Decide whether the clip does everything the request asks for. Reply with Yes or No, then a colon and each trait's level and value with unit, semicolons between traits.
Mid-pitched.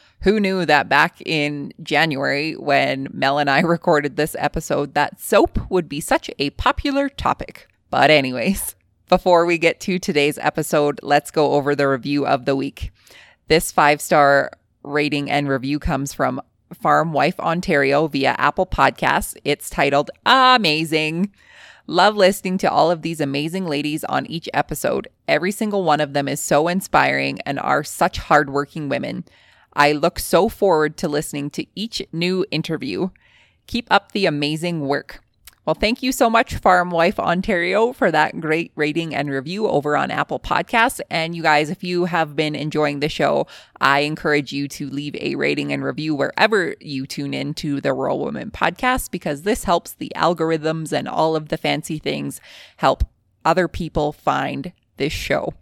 Yes: medium, 155 Hz